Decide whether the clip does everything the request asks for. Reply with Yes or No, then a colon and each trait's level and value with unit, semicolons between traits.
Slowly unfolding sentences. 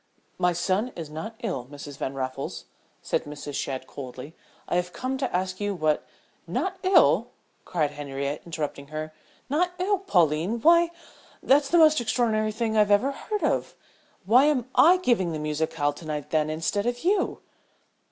No: average, 170 wpm